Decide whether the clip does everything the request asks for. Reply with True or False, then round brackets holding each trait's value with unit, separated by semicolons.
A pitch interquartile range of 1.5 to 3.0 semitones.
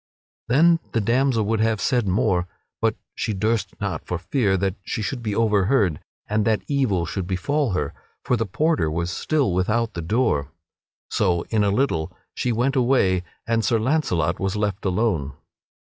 False (4.7 semitones)